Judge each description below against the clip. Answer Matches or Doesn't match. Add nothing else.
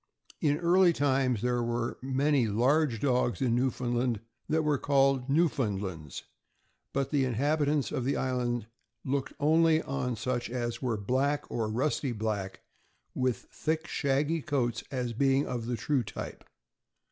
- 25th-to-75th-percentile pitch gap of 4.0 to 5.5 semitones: Doesn't match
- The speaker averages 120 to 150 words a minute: Matches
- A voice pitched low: Matches